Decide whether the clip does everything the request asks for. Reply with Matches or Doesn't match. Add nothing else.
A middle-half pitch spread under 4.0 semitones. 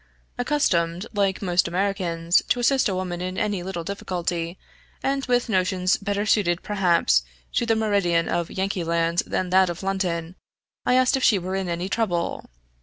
Matches